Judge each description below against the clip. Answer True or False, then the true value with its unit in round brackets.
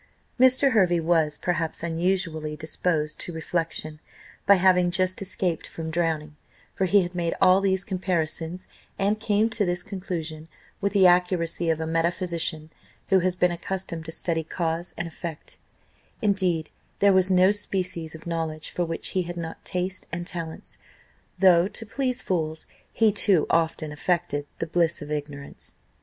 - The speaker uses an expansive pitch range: False (2.6 semitones)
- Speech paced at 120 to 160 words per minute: True (155 wpm)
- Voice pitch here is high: False (175 Hz)